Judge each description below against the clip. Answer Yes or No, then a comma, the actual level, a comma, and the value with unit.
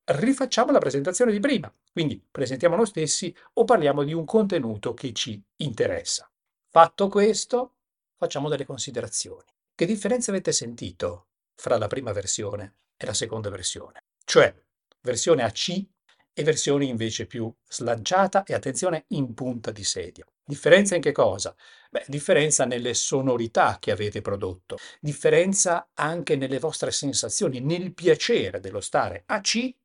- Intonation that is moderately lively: No, wide, 8.3 semitones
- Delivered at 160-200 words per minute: No, average, 140 wpm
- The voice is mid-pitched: Yes, medium, 165 Hz